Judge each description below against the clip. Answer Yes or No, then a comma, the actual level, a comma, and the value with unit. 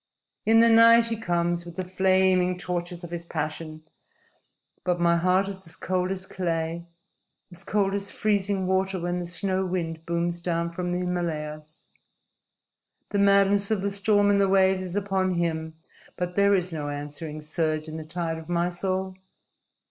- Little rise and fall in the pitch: Yes, narrow, 2.3 semitones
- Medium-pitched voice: Yes, medium, 180 Hz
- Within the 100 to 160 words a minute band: No, average, 170 wpm